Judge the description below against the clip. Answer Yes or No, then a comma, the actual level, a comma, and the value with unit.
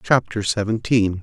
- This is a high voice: No, low, 110 Hz